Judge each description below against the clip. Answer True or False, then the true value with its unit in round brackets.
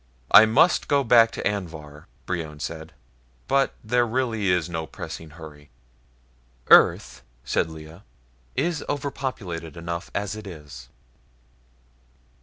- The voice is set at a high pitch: False (90 Hz)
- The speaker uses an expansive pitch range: True (6.4 semitones)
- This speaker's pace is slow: True (115 wpm)